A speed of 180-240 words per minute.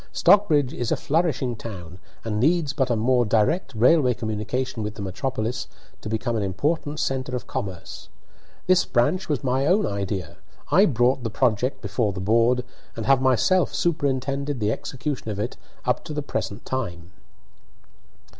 No: average, 160 wpm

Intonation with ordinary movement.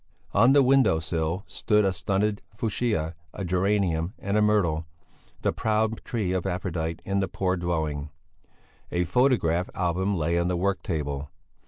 Yes: average, 4.0 semitones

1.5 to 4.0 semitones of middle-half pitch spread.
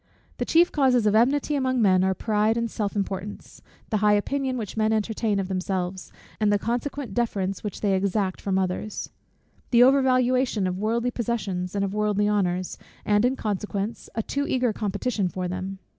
Yes: average, 3.7 semitones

